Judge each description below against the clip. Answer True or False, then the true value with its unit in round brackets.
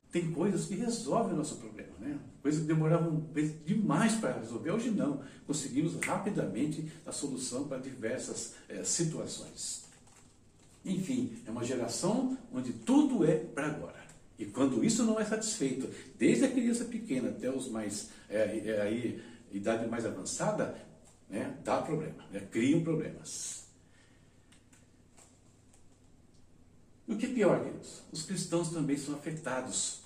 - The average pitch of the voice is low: False (165 Hz)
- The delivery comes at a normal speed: True (140 wpm)